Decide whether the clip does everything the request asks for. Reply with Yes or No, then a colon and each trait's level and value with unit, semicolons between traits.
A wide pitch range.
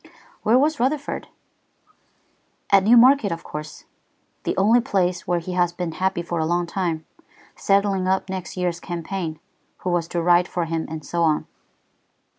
No: narrow, 2.6 semitones